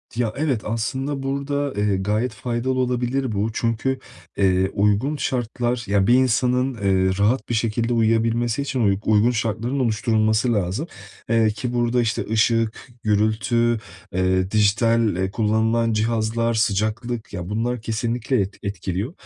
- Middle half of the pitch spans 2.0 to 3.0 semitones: Yes, average, 2.7 semitones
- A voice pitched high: No, low, 115 Hz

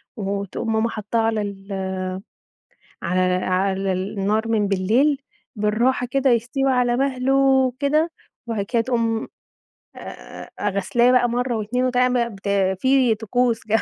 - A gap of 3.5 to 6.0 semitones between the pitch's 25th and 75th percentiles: Yes, average, 3.8 semitones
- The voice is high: Yes, high, 230 Hz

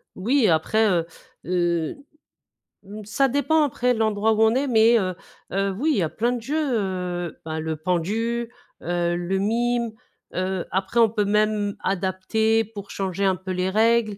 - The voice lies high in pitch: Yes, high, 205 Hz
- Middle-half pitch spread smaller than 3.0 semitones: No, average, 3.6 semitones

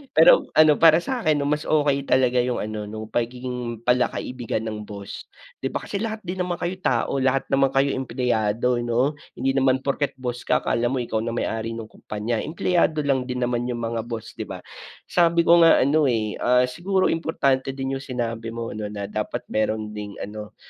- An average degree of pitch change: Yes, average, 4.0 semitones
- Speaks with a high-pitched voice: No, low, 125 Hz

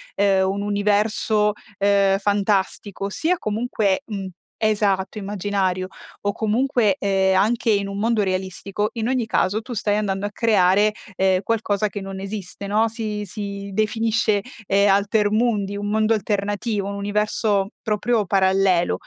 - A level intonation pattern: Yes, narrow, 1.6 semitones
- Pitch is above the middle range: Yes, high, 205 Hz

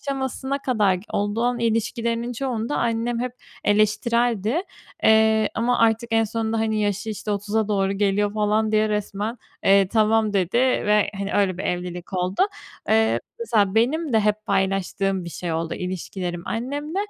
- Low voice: No, high, 215 Hz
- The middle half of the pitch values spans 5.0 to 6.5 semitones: No, average, 2.7 semitones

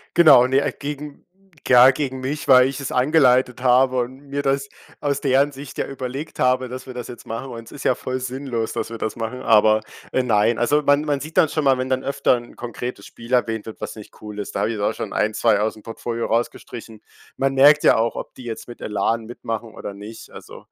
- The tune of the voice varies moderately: Yes, average, 3.1 semitones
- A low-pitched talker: Yes, low, 125 Hz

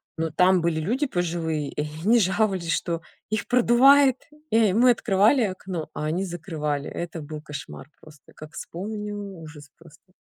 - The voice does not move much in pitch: No, average, 5.1 semitones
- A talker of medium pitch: Yes, medium, 175 Hz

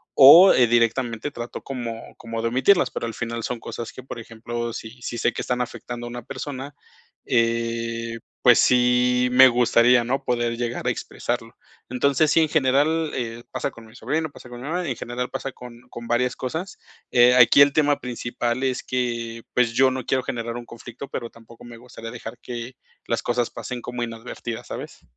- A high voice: No, low, 120 Hz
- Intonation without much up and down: Yes, narrow, 1.7 semitones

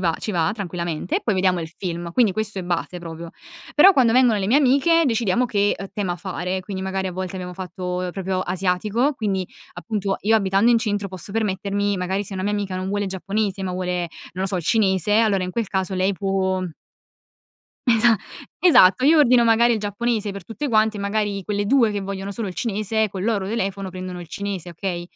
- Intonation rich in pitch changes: No, average, 2.8 semitones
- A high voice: Yes, high, 195 Hz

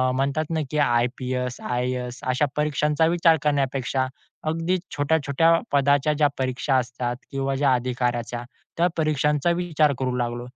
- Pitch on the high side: No, low, 135 Hz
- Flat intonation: No, average, 3.2 semitones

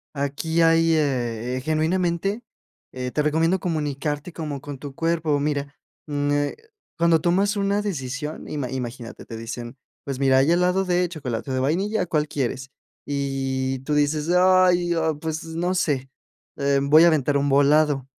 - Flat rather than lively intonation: No, average, 3.6 semitones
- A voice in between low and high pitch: Yes, medium, 150 Hz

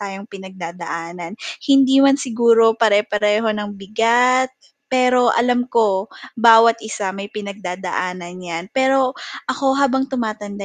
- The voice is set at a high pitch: Yes, high, 220 Hz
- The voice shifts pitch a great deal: No, average, 4.2 semitones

